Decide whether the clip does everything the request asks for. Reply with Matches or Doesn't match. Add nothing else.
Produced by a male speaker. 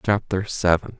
Matches